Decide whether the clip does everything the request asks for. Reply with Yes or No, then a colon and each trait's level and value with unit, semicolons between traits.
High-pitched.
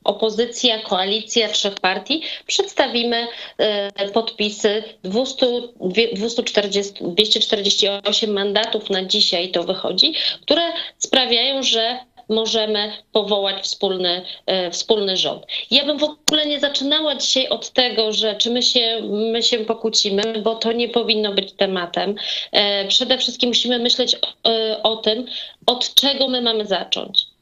Yes: high, 225 Hz